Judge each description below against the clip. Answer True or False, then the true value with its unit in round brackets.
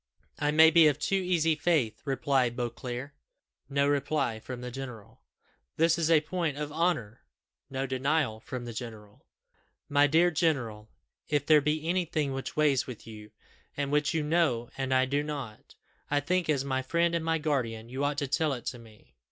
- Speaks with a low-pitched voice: False (145 Hz)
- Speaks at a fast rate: False (165 wpm)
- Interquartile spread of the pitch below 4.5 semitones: True (3.7 semitones)